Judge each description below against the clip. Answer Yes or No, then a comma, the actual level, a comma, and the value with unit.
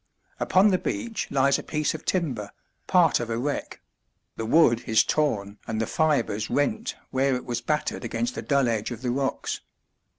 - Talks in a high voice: No, low, 135 Hz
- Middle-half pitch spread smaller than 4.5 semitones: No, wide, 5.4 semitones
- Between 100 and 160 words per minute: No, average, 185 wpm